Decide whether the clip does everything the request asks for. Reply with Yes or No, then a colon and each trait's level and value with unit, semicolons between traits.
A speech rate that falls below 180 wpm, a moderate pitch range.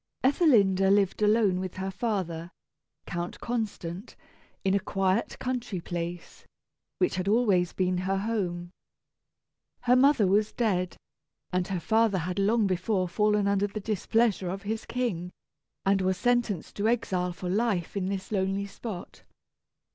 Yes: average, 140 wpm; average, 3.3 semitones